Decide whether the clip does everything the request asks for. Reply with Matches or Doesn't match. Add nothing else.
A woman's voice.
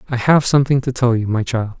Doesn't match